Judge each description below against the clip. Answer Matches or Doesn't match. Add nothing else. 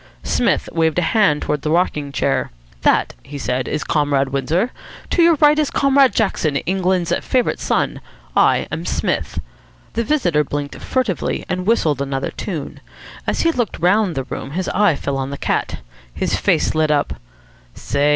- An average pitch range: Doesn't match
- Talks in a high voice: Doesn't match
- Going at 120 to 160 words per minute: Doesn't match